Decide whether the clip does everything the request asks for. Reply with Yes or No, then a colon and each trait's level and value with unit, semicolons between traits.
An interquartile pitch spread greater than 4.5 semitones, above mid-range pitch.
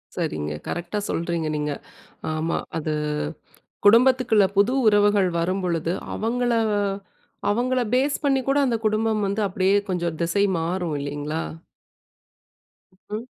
Yes: average, 5.2 semitones; high, 195 Hz